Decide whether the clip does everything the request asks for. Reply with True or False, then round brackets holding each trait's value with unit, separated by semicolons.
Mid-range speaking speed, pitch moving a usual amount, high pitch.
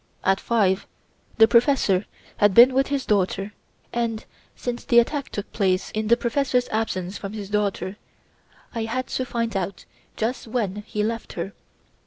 True (160 wpm; 3.2 semitones; 220 Hz)